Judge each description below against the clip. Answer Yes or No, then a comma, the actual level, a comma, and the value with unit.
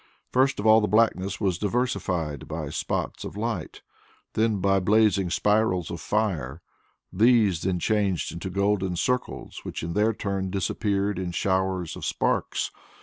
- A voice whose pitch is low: Yes, low, 100 Hz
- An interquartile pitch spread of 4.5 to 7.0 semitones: No, average, 3.0 semitones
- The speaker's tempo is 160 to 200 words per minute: No, average, 145 wpm